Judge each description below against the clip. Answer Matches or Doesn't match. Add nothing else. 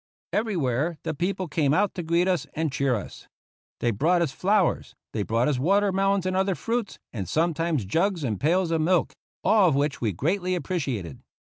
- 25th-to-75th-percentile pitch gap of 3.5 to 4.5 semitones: Doesn't match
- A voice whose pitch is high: Doesn't match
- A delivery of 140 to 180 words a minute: Doesn't match